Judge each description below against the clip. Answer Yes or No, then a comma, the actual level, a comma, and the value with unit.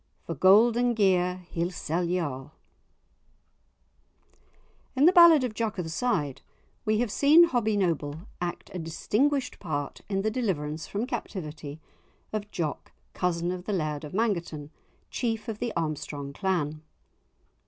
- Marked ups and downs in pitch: Yes, wide, 6.1 semitones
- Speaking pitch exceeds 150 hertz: Yes, medium, 185 Hz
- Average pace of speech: Yes, average, 145 wpm